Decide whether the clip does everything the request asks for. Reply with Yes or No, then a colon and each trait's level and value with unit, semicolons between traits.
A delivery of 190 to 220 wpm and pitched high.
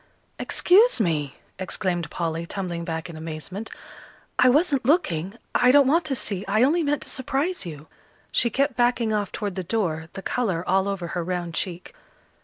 No: average, 175 wpm; high, 195 Hz